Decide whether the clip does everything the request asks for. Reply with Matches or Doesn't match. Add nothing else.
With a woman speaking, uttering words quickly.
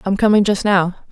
Matches